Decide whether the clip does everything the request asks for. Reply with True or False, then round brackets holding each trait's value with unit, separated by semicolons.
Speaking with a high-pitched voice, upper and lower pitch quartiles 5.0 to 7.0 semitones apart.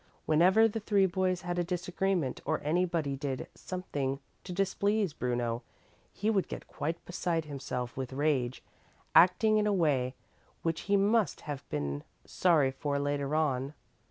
False (160 Hz; 5.4 semitones)